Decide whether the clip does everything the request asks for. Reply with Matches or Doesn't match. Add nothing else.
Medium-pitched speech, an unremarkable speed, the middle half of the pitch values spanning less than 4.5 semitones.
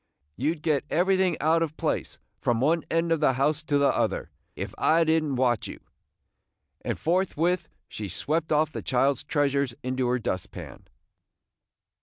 Matches